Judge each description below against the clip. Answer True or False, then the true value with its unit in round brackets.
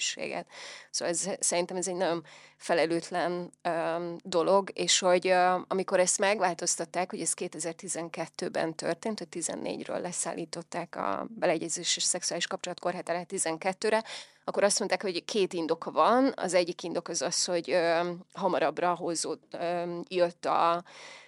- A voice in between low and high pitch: True (175 Hz)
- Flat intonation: True (1.7 semitones)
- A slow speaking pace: False (135 wpm)